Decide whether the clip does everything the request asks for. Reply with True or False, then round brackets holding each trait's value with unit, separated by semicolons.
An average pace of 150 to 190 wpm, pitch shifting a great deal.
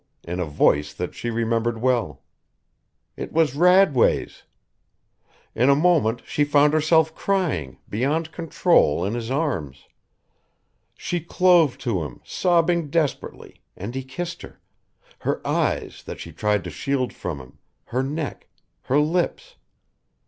False (135 wpm; 7.7 semitones)